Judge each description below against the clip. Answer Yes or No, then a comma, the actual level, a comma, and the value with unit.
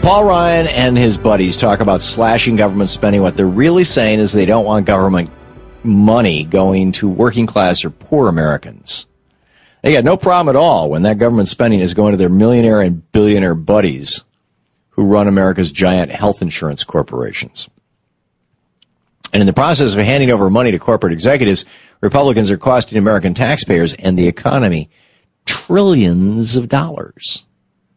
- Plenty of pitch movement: No, average, 4.2 semitones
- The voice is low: Yes, low, 105 Hz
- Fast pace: No, average, 160 wpm